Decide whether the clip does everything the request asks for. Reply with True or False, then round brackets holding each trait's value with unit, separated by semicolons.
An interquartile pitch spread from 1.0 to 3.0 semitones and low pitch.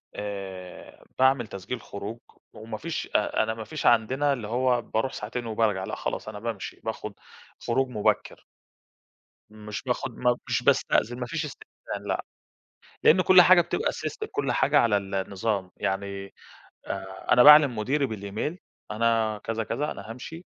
False (3.8 semitones; 115 Hz)